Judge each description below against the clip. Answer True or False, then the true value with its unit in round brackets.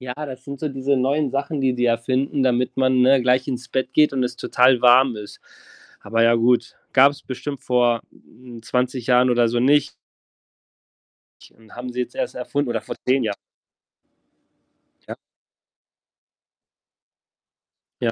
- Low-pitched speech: True (125 Hz)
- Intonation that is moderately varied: False (1.8 semitones)